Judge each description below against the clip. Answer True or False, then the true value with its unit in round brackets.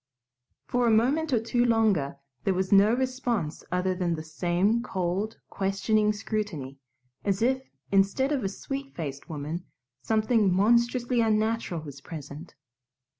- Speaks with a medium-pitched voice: False (205 Hz)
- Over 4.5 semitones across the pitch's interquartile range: True (5.1 semitones)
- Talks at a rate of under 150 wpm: True (135 wpm)